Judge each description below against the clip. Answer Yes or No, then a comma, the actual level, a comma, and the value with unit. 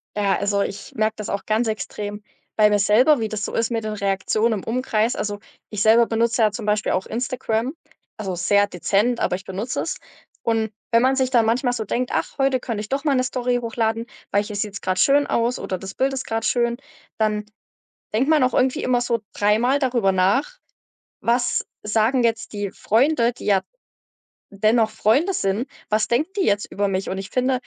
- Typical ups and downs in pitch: Yes, average, 3.2 semitones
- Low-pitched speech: No, high, 225 Hz